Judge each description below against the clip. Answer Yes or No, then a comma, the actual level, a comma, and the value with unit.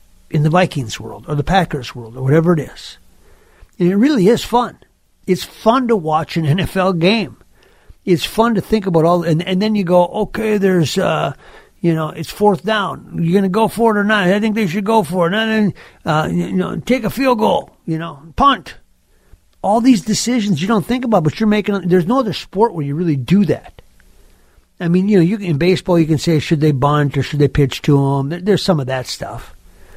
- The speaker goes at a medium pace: No, fast, 230 wpm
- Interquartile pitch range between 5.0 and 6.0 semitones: Yes, average, 5.3 semitones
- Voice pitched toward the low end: No, medium, 180 Hz